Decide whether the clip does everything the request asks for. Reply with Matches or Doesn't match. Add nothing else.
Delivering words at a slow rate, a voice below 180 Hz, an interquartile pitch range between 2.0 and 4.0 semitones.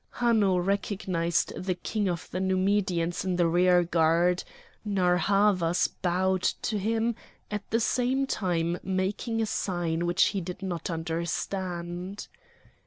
Doesn't match